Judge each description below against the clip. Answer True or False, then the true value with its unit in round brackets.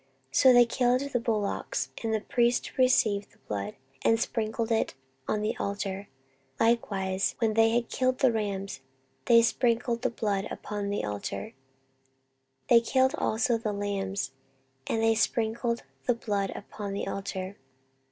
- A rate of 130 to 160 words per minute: True (150 wpm)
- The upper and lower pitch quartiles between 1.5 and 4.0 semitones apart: True (2.8 semitones)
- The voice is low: False (225 Hz)